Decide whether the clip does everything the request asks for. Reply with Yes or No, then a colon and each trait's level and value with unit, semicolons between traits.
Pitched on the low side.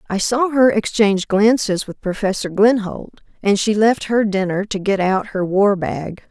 No: high, 205 Hz